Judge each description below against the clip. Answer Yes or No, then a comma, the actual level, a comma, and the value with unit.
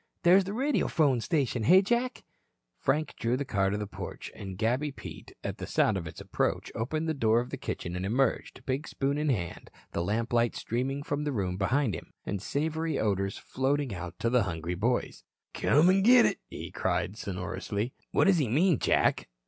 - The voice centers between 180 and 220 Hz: No, low, 125 Hz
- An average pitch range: No, wide, 6.9 semitones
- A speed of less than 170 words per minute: No, average, 195 wpm